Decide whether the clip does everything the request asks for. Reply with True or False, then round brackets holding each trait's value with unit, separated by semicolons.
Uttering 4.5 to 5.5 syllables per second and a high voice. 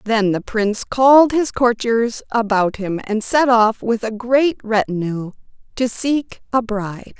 False (4.0 syllables/s; 230 Hz)